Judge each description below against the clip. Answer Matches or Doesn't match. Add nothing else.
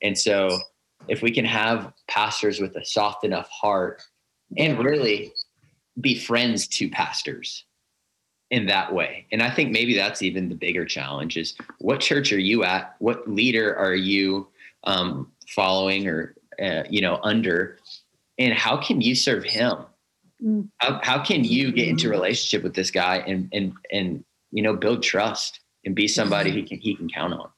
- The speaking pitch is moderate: Doesn't match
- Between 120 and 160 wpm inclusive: Doesn't match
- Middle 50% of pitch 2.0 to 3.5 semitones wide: Doesn't match